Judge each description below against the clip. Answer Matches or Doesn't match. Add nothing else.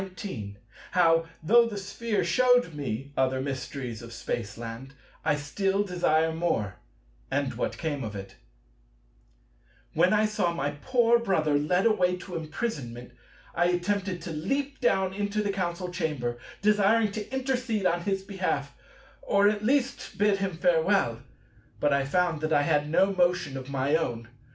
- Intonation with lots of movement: Matches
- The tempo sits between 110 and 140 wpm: Doesn't match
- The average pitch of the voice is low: Doesn't match